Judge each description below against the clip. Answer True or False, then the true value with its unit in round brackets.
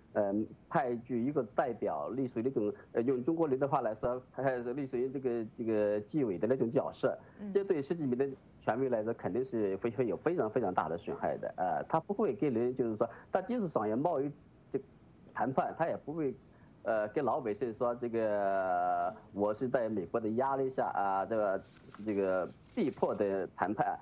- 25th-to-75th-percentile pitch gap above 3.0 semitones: True (4.4 semitones)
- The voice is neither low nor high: False (120 Hz)